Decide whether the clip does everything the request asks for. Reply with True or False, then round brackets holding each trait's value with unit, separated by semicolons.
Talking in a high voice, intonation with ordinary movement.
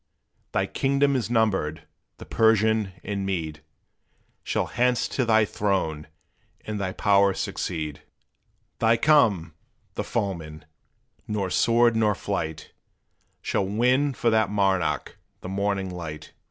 False (100 Hz; 3.8 semitones)